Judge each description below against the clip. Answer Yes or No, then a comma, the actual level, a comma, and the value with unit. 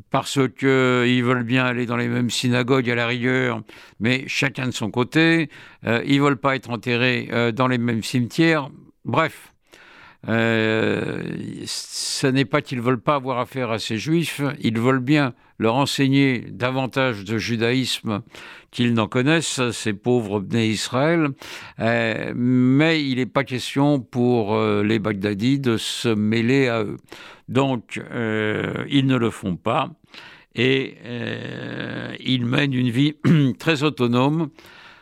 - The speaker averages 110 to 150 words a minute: Yes, slow, 145 wpm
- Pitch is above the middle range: No, low, 125 Hz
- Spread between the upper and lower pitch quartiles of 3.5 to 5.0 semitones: No, average, 3.1 semitones